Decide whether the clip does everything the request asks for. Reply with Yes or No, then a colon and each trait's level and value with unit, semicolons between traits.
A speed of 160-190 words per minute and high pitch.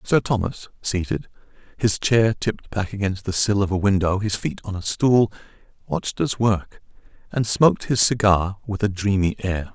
No: average, 180 wpm; low, 105 Hz